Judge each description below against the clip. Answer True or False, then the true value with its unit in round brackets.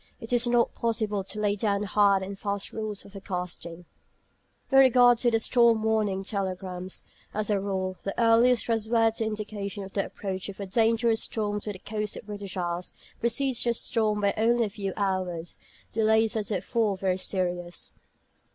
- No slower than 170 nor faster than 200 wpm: True (175 wpm)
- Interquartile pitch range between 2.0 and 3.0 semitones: True (2.7 semitones)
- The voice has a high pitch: True (210 Hz)